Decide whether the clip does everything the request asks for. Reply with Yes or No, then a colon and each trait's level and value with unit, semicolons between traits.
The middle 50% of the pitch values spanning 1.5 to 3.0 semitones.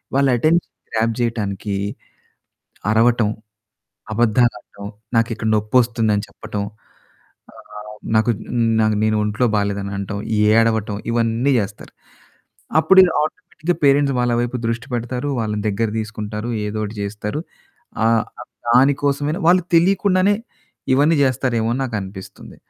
No: average, 3.7 semitones